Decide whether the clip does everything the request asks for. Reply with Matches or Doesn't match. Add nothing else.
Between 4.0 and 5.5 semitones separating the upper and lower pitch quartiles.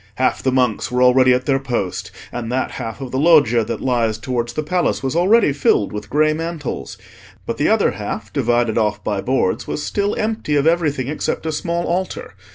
Matches